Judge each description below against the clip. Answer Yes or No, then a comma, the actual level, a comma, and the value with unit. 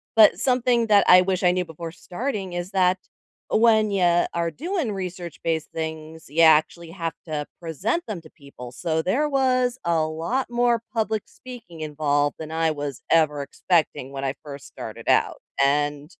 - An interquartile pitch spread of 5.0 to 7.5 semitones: Yes, wide, 5.6 semitones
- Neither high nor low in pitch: Yes, medium, 170 Hz